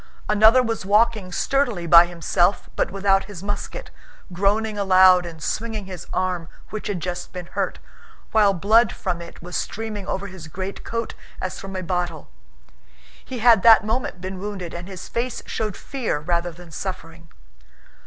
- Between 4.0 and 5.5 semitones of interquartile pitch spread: No, average, 3.4 semitones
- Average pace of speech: Yes, average, 160 wpm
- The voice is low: No, high, 190 Hz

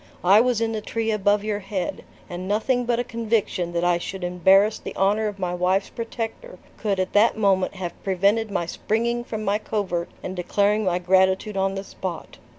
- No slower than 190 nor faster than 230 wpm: Yes, average, 195 wpm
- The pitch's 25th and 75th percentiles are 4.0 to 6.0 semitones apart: No, average, 2.8 semitones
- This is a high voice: Yes, high, 200 Hz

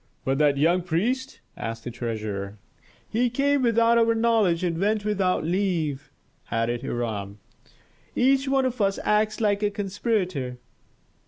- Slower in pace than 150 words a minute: Yes, average, 140 wpm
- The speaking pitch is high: Yes, high, 195 Hz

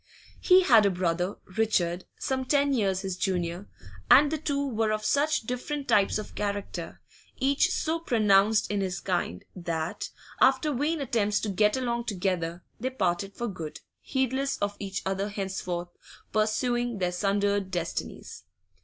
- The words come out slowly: No, average, 150 wpm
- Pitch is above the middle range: Yes, high, 205 Hz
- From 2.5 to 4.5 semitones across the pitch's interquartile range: No, wide, 5.4 semitones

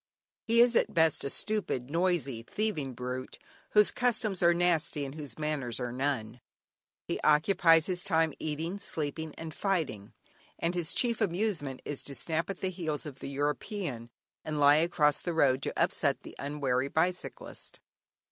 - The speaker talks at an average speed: Yes, average, 160 wpm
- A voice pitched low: No, medium, 155 Hz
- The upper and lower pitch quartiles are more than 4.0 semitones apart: Yes, average, 4.4 semitones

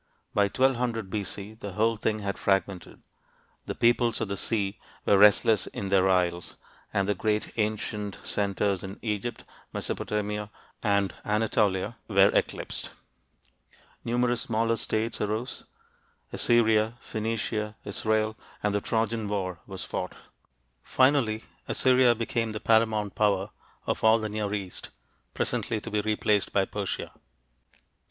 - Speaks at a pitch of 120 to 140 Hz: No, low, 105 Hz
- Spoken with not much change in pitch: Yes, narrow, 2.0 semitones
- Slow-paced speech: Yes, slow, 130 wpm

